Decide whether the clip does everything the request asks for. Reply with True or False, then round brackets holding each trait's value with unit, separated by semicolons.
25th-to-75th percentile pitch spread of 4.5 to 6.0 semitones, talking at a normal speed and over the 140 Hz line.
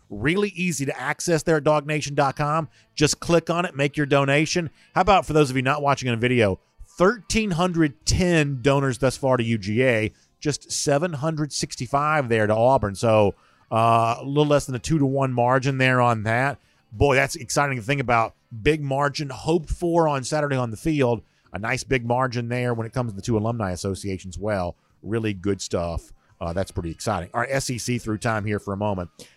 False (5.1 semitones; 195 wpm; 130 Hz)